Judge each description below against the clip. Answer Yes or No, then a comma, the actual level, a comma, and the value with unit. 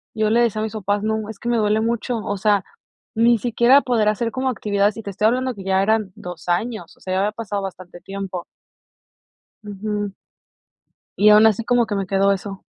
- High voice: Yes, high, 210 Hz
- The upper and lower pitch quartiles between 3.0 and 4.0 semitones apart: No, narrow, 2.4 semitones